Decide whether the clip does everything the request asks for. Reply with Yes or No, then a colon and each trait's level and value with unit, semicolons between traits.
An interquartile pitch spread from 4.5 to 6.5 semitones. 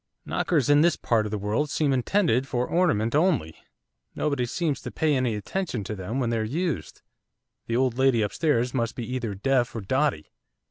Yes: average, 4.8 semitones